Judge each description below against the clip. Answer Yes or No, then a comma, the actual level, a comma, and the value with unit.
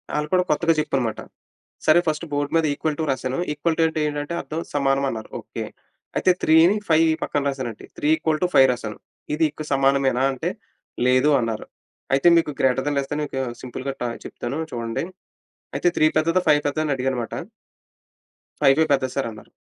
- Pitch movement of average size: Yes, average, 3.1 semitones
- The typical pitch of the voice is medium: Yes, medium, 145 Hz